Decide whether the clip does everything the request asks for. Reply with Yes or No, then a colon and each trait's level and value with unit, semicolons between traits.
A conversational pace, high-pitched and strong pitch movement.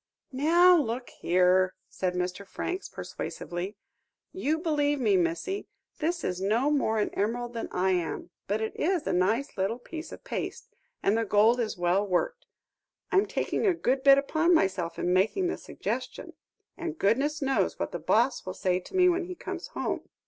Yes: average, 180 wpm; high, 240 Hz; wide, 9.0 semitones